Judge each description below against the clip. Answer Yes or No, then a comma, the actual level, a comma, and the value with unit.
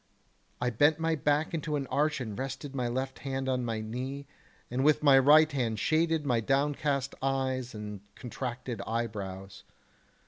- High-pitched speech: No, low, 135 Hz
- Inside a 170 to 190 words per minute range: No, average, 160 wpm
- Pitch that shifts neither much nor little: Yes, average, 3.4 semitones